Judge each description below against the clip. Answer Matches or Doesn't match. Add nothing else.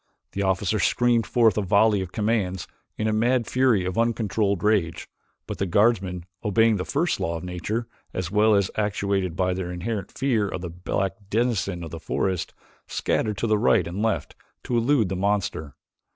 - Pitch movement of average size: Matches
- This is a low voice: Matches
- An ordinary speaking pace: Matches